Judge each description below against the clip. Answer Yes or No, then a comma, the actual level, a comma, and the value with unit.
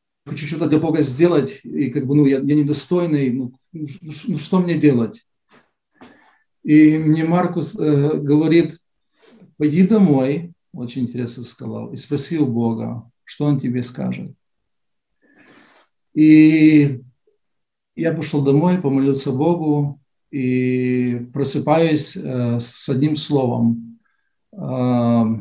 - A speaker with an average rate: Yes, average, 120 wpm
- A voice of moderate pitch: Yes, medium, 145 Hz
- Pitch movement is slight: No, average, 3.6 semitones